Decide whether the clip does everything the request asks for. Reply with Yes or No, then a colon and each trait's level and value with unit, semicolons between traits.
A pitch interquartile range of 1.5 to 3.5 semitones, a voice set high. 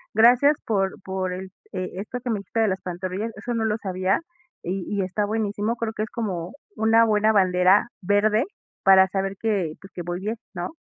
Yes: average, 2.8 semitones; high, 205 Hz